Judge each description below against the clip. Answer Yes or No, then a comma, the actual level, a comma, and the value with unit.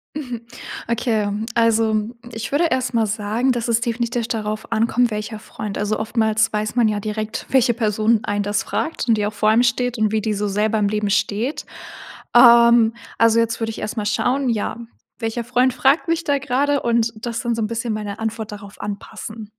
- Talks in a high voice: Yes, high, 225 Hz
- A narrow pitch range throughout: Yes, narrow, 2.1 semitones